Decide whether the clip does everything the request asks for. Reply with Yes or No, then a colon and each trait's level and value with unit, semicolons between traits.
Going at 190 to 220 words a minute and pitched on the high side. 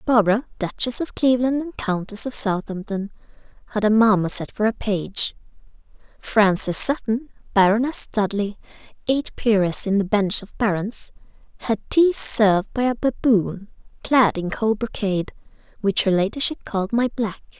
No: average, 140 wpm; high, 215 Hz